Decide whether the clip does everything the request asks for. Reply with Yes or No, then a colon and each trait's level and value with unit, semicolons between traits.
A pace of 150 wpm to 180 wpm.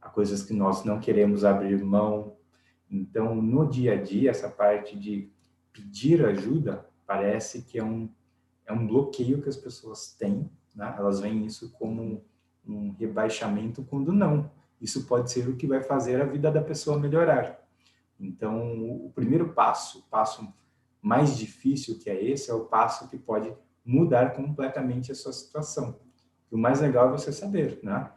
Yes: average, 170 wpm